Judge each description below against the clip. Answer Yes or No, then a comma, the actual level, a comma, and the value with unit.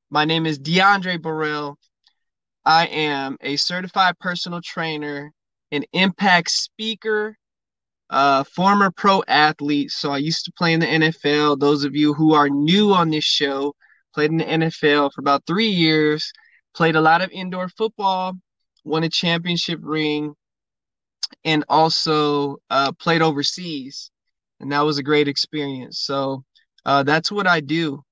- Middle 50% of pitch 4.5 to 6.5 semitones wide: No, average, 3.5 semitones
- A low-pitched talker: No, medium, 155 Hz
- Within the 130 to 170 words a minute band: Yes, average, 150 wpm